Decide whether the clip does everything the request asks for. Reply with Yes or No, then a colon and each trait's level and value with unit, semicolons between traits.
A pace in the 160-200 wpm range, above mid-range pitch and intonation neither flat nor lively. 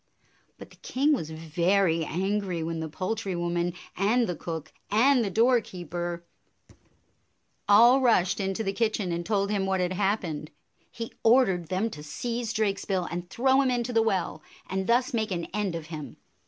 Yes: average, 170 wpm; high, 195 Hz; average, 4.6 semitones